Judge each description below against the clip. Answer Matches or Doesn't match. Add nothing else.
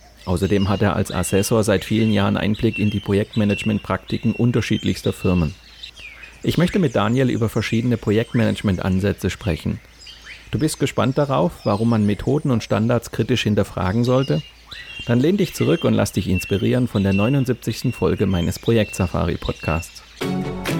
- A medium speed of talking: Matches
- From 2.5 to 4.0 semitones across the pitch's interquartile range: Matches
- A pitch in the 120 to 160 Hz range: Doesn't match